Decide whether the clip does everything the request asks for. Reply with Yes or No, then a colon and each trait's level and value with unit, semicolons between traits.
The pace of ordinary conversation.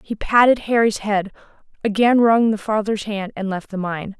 Yes: average, 185 wpm